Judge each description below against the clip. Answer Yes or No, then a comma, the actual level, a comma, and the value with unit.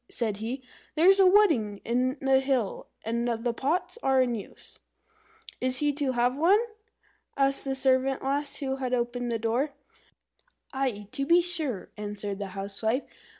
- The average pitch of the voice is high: Yes, very high, 255 Hz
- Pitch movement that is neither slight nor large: Yes, average, 3.3 semitones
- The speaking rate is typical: Yes, average, 160 wpm